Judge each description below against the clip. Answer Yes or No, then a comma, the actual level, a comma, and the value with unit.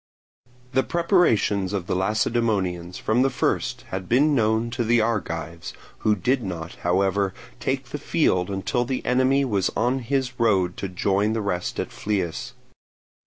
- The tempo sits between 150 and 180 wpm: Yes, average, 155 wpm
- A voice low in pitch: Yes, low, 110 Hz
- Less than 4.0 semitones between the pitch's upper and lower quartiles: No, average, 4.8 semitones